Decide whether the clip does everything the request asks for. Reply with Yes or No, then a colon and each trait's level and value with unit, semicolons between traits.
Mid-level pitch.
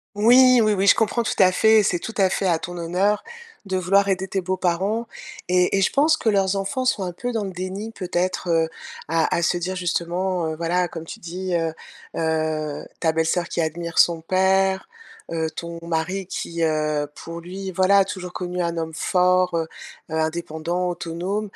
Yes: medium, 180 Hz